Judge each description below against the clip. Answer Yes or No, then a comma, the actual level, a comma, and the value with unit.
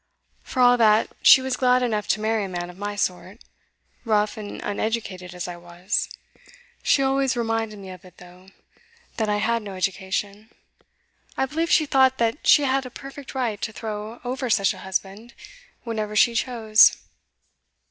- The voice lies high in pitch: Yes, high, 220 Hz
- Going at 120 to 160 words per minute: No, average, 170 wpm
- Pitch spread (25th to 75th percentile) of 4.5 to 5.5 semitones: No, average, 4.0 semitones